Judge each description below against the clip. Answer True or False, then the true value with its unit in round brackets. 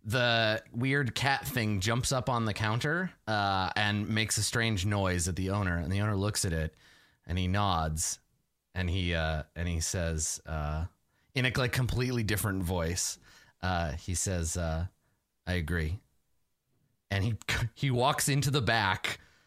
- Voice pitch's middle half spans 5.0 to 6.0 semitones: True (5.3 semitones)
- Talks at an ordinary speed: True (165 wpm)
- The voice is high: False (100 Hz)